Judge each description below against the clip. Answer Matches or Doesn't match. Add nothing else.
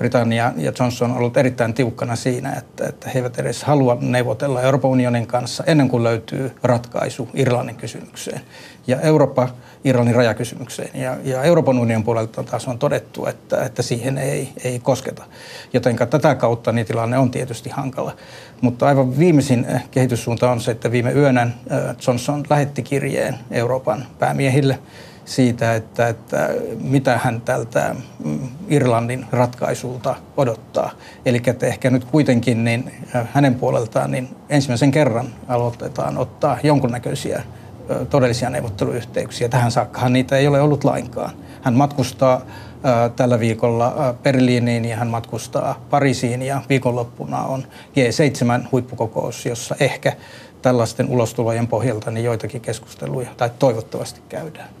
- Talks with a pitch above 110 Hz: Matches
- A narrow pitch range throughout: Matches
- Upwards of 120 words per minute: Matches